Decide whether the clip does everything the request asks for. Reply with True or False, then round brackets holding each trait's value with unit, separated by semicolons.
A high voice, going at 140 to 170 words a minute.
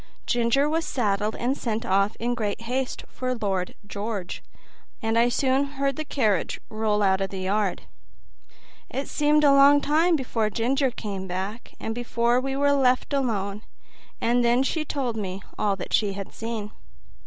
True (235 Hz; 165 wpm)